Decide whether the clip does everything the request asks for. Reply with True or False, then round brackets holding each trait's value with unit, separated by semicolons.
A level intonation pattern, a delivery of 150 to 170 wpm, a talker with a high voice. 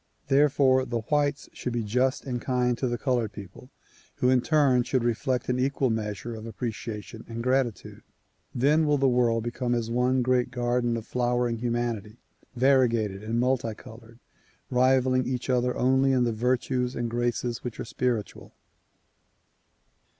False (1.8 semitones; 155 wpm; 125 Hz)